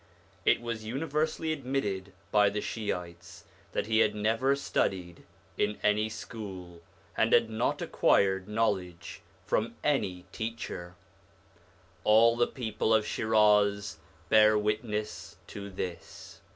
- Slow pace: Yes, slow, 115 wpm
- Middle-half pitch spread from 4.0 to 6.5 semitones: No, average, 2.8 semitones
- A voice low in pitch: Yes, low, 105 Hz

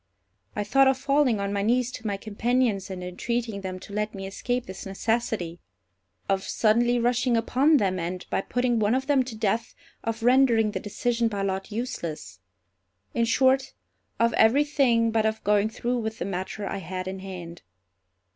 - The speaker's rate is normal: Yes, average, 175 wpm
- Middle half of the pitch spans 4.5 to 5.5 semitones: No, average, 4.0 semitones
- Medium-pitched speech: No, high, 220 Hz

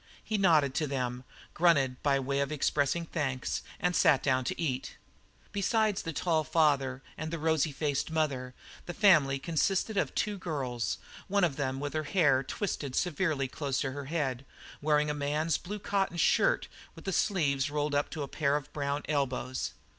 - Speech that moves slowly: No, average, 180 wpm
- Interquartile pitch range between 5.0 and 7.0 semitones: No, average, 3.6 semitones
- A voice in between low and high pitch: Yes, medium, 150 Hz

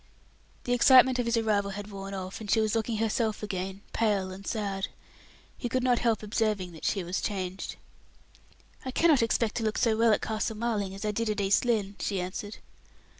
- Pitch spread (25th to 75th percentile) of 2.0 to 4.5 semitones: Yes, average, 2.7 semitones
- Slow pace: No, average, 200 wpm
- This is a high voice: Yes, high, 215 Hz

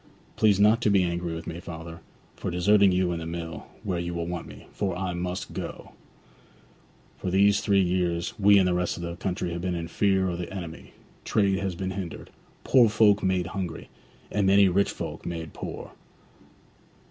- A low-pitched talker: Yes, very low, 90 Hz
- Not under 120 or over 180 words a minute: No, average, 190 wpm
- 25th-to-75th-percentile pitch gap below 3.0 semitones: Yes, narrow, 2.4 semitones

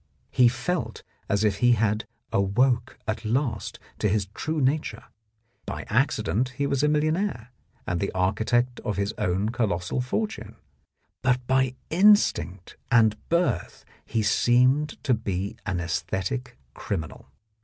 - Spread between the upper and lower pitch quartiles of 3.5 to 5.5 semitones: Yes, average, 4.7 semitones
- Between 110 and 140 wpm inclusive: Yes, slow, 135 wpm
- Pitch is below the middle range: Yes, low, 115 Hz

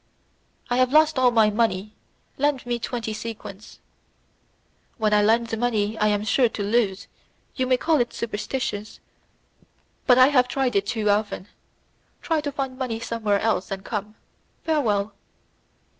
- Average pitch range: Yes, average, 3.5 semitones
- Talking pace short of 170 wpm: Yes, average, 150 wpm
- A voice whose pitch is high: Yes, high, 230 Hz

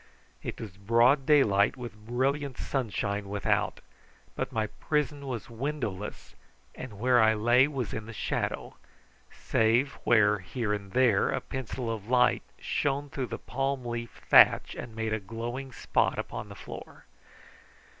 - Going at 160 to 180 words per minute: No, average, 145 wpm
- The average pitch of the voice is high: No, low, 120 Hz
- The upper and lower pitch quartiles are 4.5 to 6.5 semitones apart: No, average, 3.8 semitones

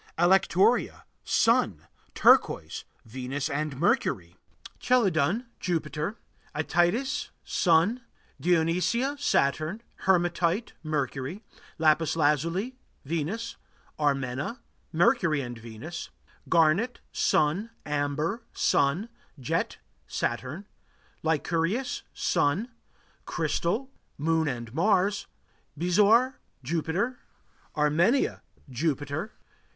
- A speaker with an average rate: No, slow, 75 wpm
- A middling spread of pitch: No, wide, 5.8 semitones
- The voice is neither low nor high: Yes, medium, 165 Hz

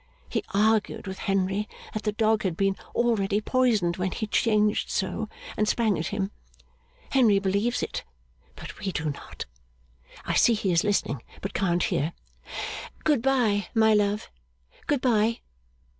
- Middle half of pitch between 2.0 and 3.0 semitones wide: Yes, narrow, 2.5 semitones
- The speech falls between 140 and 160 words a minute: Yes, average, 150 wpm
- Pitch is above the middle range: Yes, high, 210 Hz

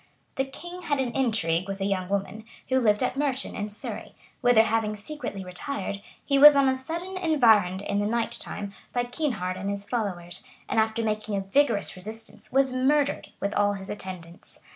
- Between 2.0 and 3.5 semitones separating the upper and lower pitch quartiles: No, average, 5.1 semitones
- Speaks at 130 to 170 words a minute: No, average, 185 wpm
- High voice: Yes, high, 220 Hz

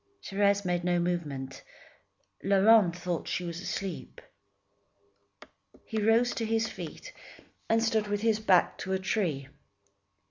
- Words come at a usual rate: No, slow, 130 wpm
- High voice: Yes, high, 195 Hz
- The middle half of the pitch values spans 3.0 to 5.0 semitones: Yes, average, 4.0 semitones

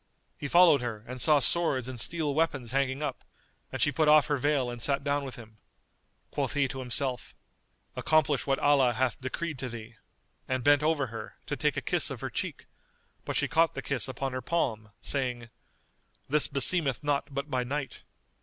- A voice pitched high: No, low, 135 Hz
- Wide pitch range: No, average, 2.9 semitones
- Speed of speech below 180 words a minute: No, average, 190 wpm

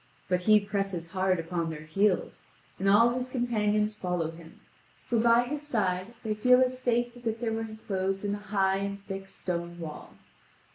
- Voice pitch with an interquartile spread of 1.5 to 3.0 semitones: No, average, 4.1 semitones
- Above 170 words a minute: Yes, average, 185 wpm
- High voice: Yes, high, 205 Hz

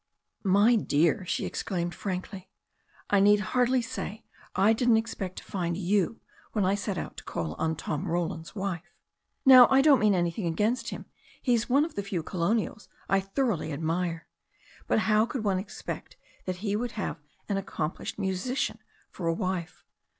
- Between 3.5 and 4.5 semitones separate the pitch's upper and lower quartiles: Yes, average, 4.2 semitones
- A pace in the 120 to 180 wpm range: Yes, average, 165 wpm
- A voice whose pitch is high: Yes, high, 195 Hz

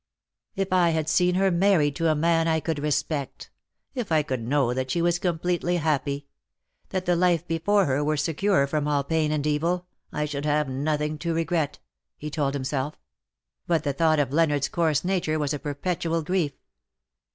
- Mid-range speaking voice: Yes, medium, 155 Hz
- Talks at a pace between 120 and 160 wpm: No, average, 185 wpm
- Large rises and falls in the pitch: No, average, 2.8 semitones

